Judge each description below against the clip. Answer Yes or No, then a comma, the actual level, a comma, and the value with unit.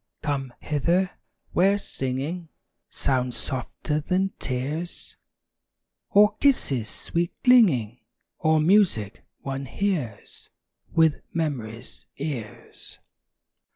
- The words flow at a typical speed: No, slow, 85 wpm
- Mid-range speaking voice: Yes, medium, 150 Hz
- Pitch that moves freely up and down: Yes, wide, 5.8 semitones